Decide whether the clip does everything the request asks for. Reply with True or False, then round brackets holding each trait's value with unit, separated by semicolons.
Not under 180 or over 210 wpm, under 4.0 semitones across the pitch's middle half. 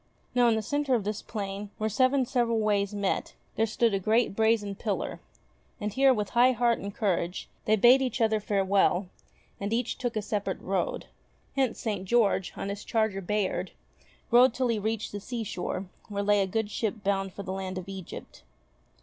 True (190 wpm; 2.9 semitones)